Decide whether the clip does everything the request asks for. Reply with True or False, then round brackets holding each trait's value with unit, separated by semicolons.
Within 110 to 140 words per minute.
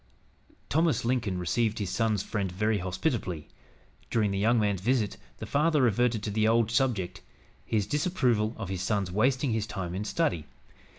False (165 wpm)